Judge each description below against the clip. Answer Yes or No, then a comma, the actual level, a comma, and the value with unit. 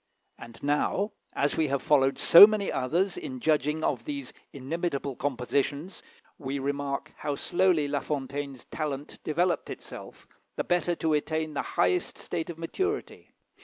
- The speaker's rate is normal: Yes, average, 145 wpm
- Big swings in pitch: No, average, 3.8 semitones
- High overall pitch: No, medium, 150 Hz